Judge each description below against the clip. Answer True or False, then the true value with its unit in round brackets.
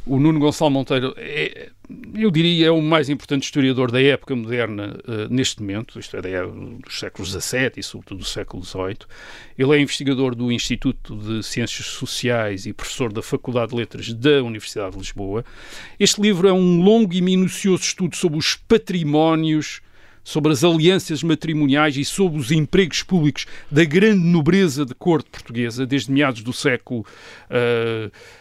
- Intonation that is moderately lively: False (5.7 semitones)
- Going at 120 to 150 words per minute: False (165 wpm)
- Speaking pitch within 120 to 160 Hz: True (135 Hz)